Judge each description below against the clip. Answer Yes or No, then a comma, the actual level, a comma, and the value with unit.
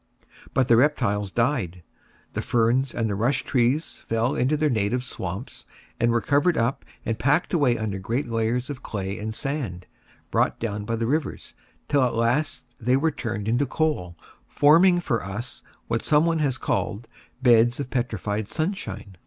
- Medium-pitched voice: No, low, 120 Hz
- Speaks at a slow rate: No, average, 165 wpm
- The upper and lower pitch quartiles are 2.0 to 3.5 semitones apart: No, average, 4.4 semitones